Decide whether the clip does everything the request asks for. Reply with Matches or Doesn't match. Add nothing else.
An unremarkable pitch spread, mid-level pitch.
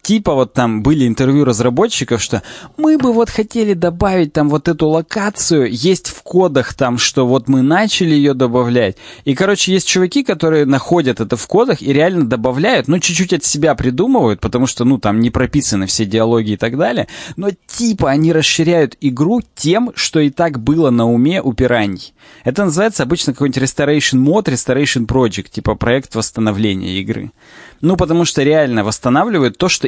Doesn't match